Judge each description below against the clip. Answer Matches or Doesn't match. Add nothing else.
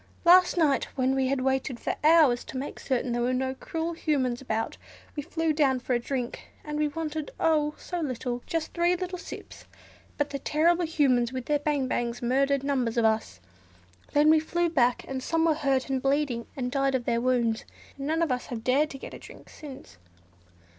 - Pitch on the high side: Matches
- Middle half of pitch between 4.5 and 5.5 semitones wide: Doesn't match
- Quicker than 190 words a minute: Matches